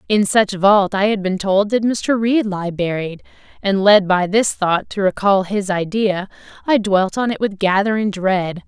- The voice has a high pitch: Yes, high, 200 Hz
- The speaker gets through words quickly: No, average, 195 wpm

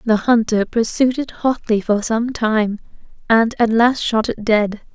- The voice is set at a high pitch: Yes, high, 225 Hz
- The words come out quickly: No, average, 170 wpm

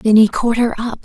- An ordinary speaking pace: No, fast, 290 wpm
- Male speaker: No, female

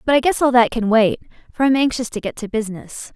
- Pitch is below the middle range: No, high, 235 Hz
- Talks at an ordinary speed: No, fast, 265 wpm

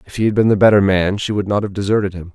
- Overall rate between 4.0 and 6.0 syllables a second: No, 7.1 syllables/s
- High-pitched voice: No, low, 100 Hz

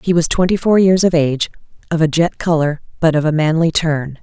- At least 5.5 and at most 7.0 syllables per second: Yes, 5.7 syllables/s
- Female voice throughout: Yes, female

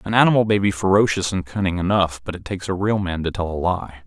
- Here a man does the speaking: Yes, male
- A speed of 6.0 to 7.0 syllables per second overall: Yes, 6.5 syllables/s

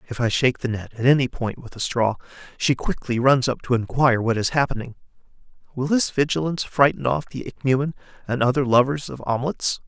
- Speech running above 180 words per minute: Yes, average, 195 wpm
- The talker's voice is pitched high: No, low, 130 Hz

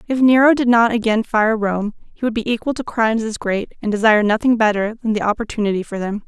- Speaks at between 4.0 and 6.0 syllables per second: No, 6.2 syllables/s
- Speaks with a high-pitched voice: Yes, high, 220 Hz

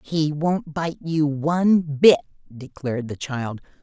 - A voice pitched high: No, medium, 150 Hz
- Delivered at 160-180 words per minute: No, average, 140 wpm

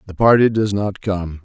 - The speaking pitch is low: Yes, low, 100 Hz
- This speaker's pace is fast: Yes, fast, 210 wpm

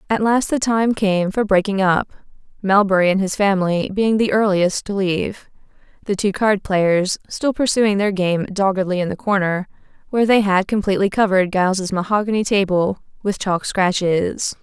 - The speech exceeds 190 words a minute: No, average, 165 wpm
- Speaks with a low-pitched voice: No, high, 195 Hz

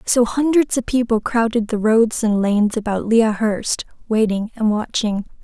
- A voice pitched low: No, high, 225 Hz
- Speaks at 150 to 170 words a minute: Yes, average, 165 wpm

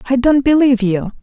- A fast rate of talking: No, average, 195 wpm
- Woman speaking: Yes, female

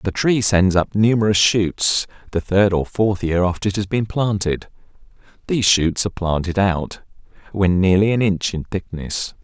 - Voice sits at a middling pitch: No, low, 100 Hz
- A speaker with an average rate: Yes, average, 170 wpm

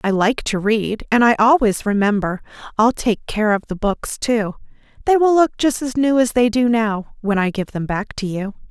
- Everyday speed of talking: No, fast, 220 wpm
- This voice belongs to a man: No, female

